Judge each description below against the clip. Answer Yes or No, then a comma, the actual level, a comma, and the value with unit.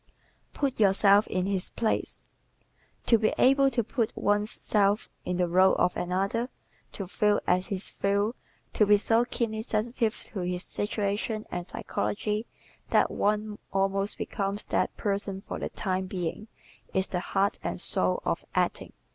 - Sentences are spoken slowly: No, average, 155 wpm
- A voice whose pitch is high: Yes, high, 205 Hz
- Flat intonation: Yes, narrow, 2.3 semitones